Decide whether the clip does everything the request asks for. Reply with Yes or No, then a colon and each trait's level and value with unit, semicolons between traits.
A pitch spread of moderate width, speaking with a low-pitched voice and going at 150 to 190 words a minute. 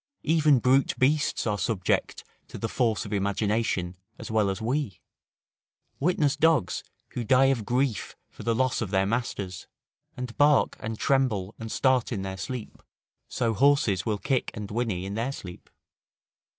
Yes: average, 4.7 semitones; low, 115 Hz; average, 160 wpm